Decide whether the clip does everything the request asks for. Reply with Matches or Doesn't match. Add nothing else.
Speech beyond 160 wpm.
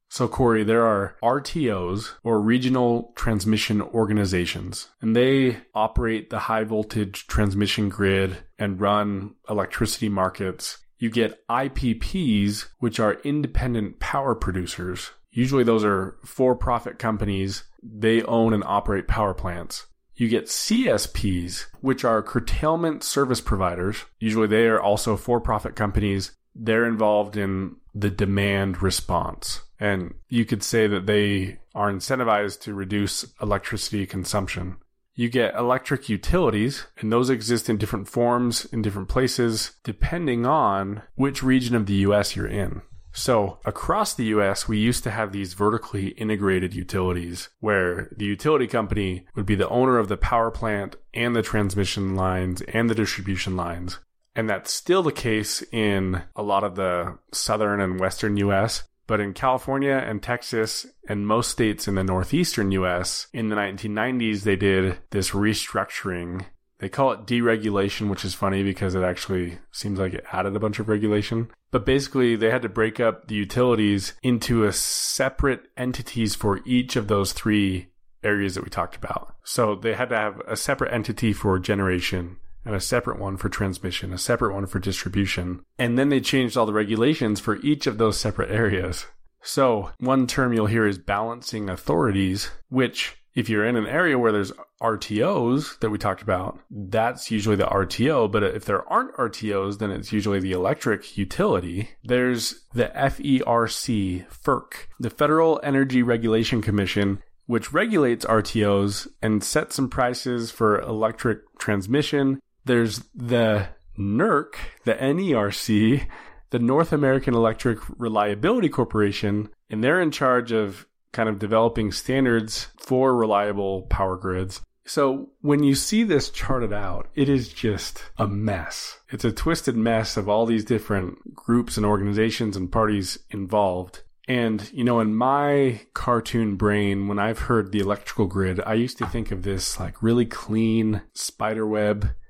Doesn't match